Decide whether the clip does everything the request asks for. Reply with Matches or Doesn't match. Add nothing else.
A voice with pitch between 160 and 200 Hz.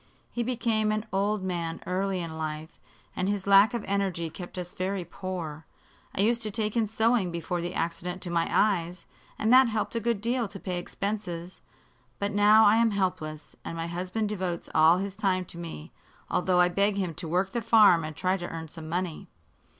Matches